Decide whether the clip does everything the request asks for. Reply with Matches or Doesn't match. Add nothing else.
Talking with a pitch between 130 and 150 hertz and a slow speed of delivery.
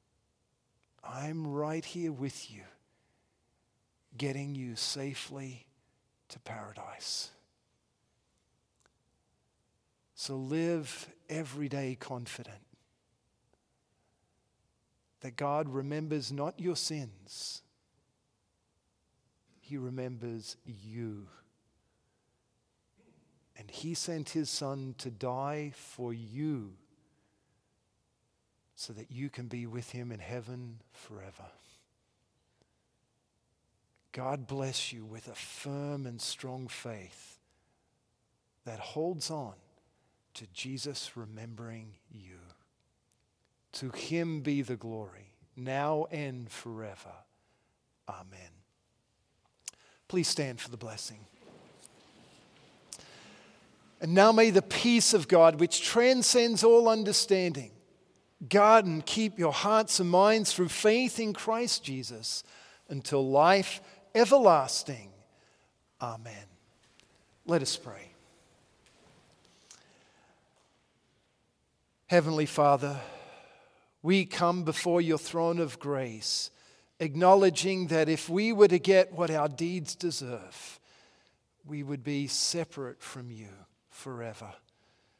Matches